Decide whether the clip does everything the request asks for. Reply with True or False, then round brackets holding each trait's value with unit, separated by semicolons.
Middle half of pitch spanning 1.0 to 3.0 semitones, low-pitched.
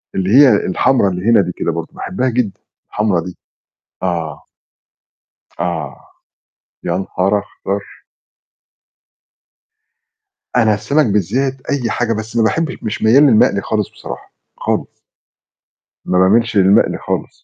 False (4.3 semitones; 105 Hz)